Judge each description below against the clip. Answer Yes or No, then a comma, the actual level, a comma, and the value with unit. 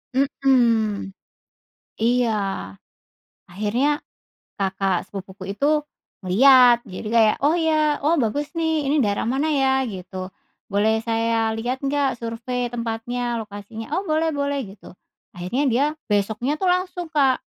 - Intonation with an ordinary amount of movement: Yes, average, 4.9 semitones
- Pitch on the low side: No, high, 240 Hz